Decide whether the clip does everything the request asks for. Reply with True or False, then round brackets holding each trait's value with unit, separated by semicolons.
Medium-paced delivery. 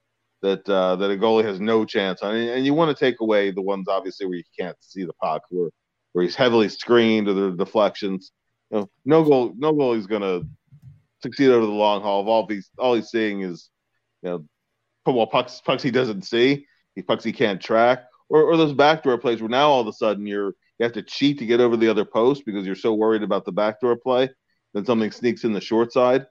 False (235 wpm)